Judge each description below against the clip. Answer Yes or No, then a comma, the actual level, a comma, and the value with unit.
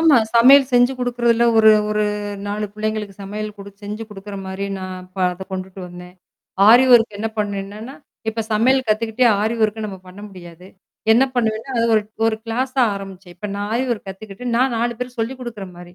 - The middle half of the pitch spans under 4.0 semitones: Yes, average, 3.3 semitones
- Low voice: No, high, 215 Hz